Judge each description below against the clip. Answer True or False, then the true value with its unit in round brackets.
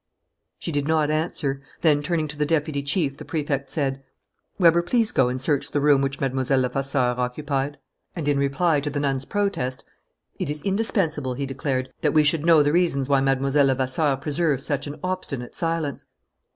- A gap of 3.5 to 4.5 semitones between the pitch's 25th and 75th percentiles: False (2.6 semitones)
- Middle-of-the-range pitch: True (145 Hz)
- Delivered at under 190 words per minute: True (180 wpm)